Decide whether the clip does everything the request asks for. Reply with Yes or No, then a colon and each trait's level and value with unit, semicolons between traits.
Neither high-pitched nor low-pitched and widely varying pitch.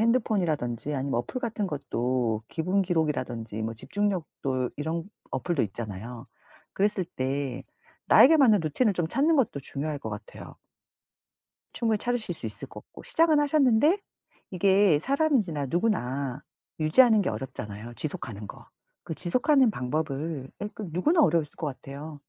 Yes: medium, 160 Hz; wide, 8.6 semitones